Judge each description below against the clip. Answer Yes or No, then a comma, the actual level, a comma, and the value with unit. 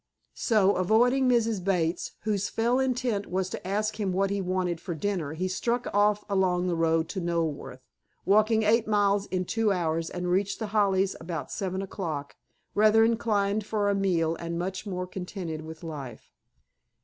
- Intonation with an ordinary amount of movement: Yes, average, 3.4 semitones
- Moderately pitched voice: No, high, 195 Hz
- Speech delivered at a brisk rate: No, average, 175 wpm